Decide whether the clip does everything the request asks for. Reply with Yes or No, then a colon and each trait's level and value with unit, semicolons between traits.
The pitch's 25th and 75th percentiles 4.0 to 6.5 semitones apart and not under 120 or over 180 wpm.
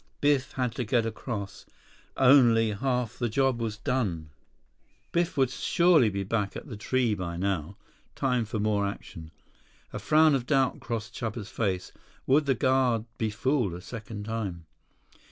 Yes: average, 4.3 semitones; average, 155 wpm